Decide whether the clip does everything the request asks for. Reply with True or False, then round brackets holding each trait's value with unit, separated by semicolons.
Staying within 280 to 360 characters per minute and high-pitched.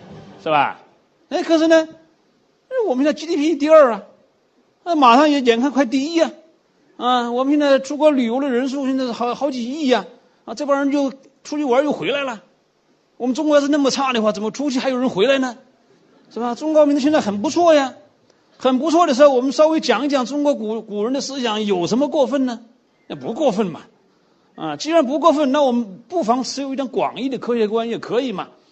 True (305 characters per minute; 275 Hz)